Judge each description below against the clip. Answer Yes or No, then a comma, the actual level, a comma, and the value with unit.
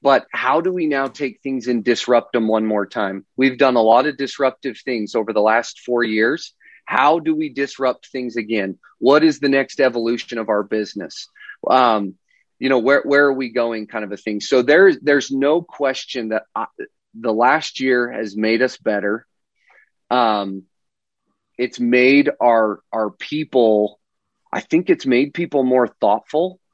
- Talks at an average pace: Yes, average, 175 wpm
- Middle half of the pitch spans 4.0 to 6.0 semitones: Yes, average, 4.3 semitones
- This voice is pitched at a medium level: No, low, 130 Hz